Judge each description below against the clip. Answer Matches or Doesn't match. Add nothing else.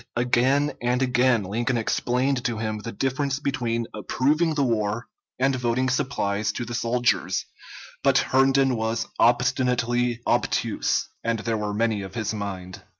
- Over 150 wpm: Doesn't match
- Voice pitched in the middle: Doesn't match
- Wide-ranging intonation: Doesn't match